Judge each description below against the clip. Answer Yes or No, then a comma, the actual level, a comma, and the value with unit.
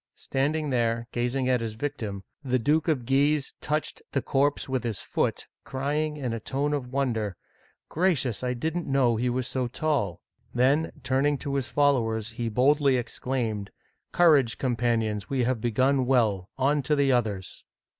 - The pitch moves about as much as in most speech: Yes, average, 3.4 semitones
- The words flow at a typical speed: Yes, average, 175 wpm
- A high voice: No, low, 130 Hz